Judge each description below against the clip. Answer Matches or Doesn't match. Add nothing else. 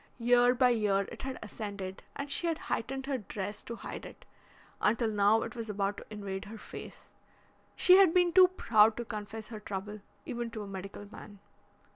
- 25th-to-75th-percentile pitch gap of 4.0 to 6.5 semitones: Doesn't match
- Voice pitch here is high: Matches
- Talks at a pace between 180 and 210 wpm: Matches